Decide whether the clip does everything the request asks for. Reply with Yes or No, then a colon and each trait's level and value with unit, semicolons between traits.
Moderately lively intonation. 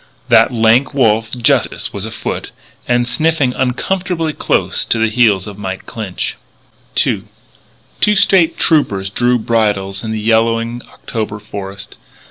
Yes: average, 3.6 semitones